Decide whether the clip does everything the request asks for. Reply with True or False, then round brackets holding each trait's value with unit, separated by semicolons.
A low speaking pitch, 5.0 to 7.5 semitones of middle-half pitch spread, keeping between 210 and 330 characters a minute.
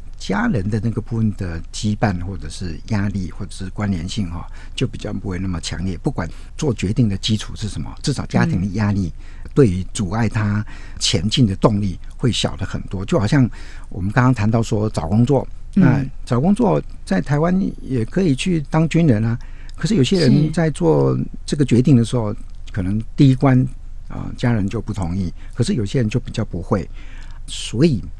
True (105 Hz; 5.4 semitones; 275 characters per minute)